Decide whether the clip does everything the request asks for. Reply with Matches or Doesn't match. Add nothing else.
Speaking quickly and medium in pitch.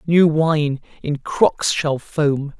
Doesn't match